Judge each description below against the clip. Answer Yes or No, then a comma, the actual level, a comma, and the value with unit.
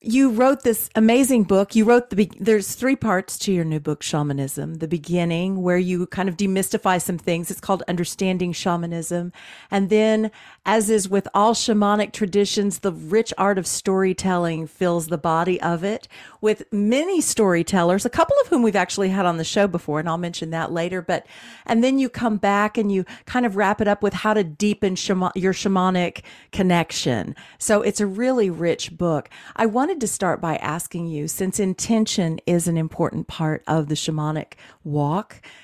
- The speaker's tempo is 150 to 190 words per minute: Yes, average, 185 wpm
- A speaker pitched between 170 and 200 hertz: Yes, high, 190 Hz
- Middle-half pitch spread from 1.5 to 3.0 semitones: No, average, 3.8 semitones